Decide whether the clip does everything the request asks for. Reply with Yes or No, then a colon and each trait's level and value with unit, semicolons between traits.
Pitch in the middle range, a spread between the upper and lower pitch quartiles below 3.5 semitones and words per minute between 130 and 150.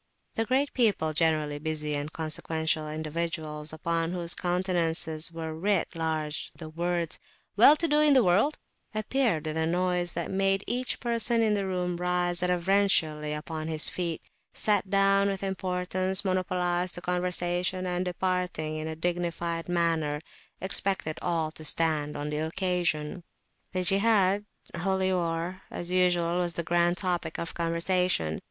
Yes: medium, 175 Hz; average, 2.7 semitones; average, 145 wpm